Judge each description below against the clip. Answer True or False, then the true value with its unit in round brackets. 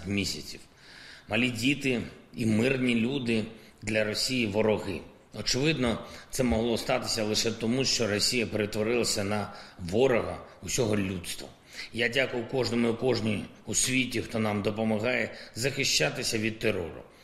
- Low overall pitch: True (110 Hz)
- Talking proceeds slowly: False (120 wpm)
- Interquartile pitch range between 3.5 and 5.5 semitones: False (2.8 semitones)